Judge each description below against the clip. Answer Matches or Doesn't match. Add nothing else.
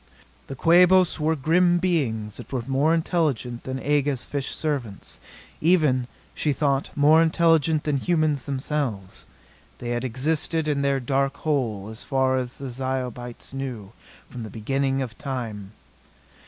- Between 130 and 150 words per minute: Matches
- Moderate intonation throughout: Matches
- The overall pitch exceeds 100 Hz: Matches